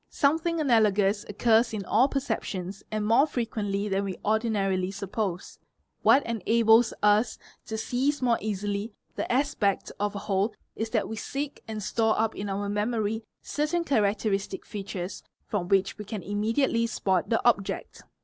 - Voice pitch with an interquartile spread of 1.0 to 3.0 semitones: Yes, narrow, 2.6 semitones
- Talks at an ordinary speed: Yes, average, 150 wpm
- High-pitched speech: Yes, high, 215 Hz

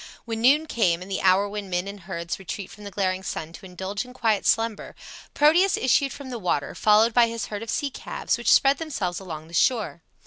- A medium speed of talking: No, fast, 220 wpm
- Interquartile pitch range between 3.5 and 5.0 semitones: Yes, average, 4.6 semitones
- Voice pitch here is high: Yes, high, 205 Hz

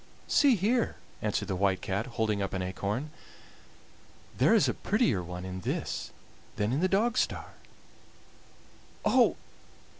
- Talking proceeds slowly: Yes, slow, 130 wpm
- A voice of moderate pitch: No, low, 105 Hz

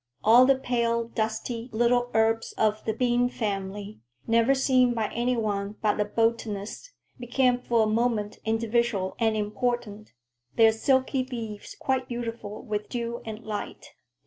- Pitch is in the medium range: No, high, 230 Hz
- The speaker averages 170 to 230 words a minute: No, average, 145 wpm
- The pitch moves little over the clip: Yes, narrow, 2.3 semitones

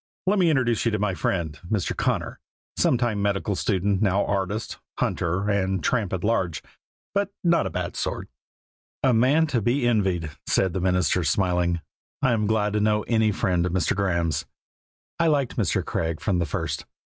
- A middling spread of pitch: Yes, average, 4.2 semitones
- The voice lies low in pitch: Yes, low, 100 Hz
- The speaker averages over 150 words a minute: Yes, average, 170 wpm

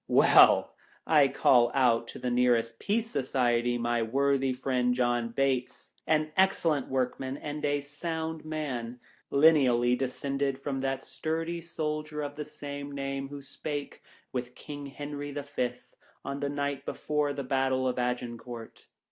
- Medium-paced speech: Yes, average, 150 wpm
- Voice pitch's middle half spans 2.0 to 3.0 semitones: Yes, average, 2.7 semitones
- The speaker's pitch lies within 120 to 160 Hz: Yes, low, 135 Hz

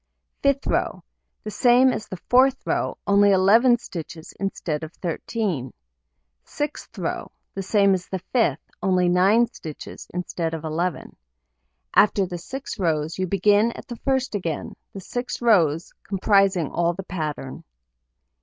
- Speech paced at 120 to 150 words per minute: Yes, average, 145 wpm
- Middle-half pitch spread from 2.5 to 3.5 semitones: No, average, 4.9 semitones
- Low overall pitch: No, high, 190 Hz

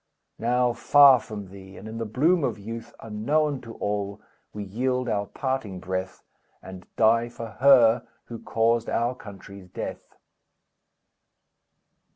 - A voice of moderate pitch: No, low, 115 Hz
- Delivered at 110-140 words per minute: Yes, slow, 135 wpm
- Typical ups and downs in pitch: Yes, average, 3.6 semitones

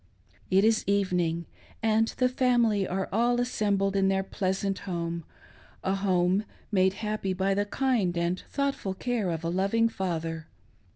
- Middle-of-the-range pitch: No, high, 195 Hz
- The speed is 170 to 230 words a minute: No, average, 160 wpm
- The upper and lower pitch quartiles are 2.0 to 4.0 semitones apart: Yes, average, 3.2 semitones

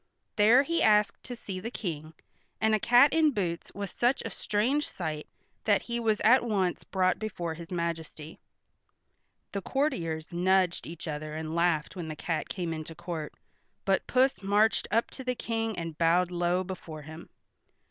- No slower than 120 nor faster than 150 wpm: No, average, 170 wpm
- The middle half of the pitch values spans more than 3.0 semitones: Yes, average, 5.0 semitones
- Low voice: No, medium, 185 Hz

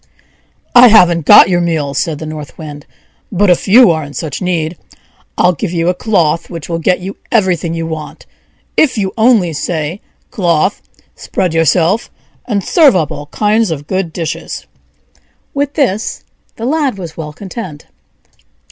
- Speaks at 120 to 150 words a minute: No, average, 160 wpm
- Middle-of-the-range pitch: Yes, medium, 175 Hz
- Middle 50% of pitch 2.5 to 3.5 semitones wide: No, average, 4.4 semitones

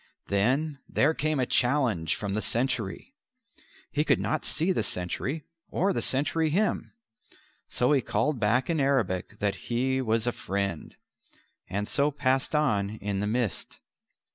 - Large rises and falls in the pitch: Yes, wide, 6.1 semitones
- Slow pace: No, average, 150 wpm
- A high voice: No, low, 125 Hz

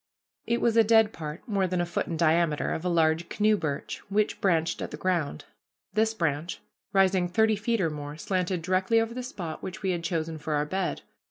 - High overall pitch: No, medium, 180 Hz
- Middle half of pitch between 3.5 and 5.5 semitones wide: Yes, average, 4.5 semitones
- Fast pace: Yes, fast, 210 wpm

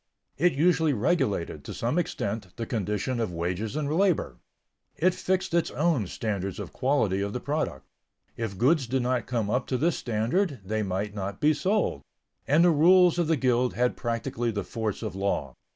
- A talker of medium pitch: No, low, 125 Hz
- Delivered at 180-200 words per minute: Yes, average, 185 wpm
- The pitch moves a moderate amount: No, wide, 7.2 semitones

